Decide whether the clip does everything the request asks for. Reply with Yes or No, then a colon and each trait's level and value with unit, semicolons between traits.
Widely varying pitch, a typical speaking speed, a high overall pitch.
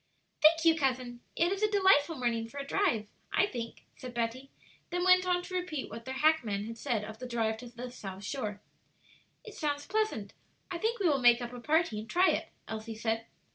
No: wide, 6.8 semitones; fast, 215 wpm; very high, 255 Hz